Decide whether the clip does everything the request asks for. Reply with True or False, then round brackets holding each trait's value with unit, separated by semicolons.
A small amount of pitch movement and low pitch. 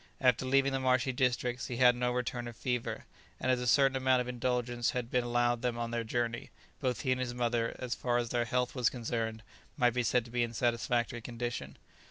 True (1.1 semitones; 120 Hz)